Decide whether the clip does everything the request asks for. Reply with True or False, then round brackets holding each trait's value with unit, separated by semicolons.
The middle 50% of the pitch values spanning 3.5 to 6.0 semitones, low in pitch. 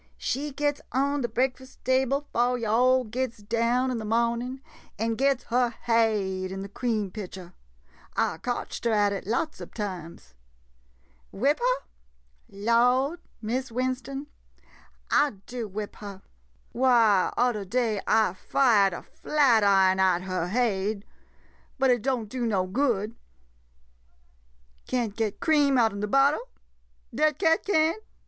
False (4.1 semitones; 235 Hz)